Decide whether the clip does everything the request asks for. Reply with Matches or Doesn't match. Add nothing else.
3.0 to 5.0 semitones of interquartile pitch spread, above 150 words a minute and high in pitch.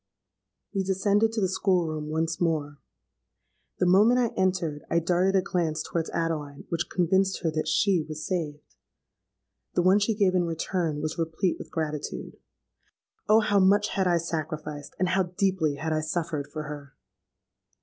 Doesn't match